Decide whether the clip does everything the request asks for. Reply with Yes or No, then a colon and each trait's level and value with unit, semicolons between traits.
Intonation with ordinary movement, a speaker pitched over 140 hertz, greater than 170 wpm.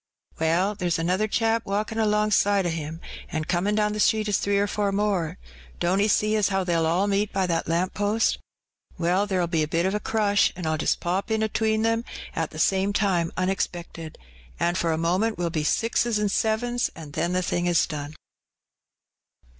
Yes: average, 3.7 semitones; high, 190 Hz; average, 195 wpm